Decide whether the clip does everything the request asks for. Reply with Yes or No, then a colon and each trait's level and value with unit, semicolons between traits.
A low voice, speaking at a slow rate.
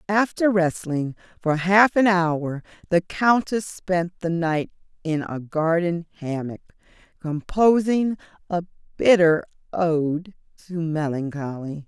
No: medium, 170 Hz; slow, 105 wpm